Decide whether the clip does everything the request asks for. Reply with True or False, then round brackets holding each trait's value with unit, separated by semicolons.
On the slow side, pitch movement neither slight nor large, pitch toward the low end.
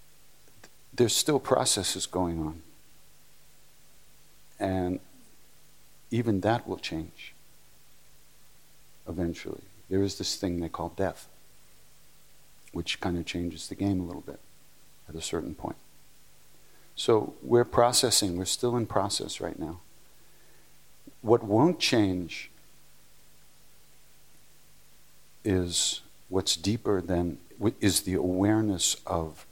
True (105 wpm; 3.1 semitones; 95 Hz)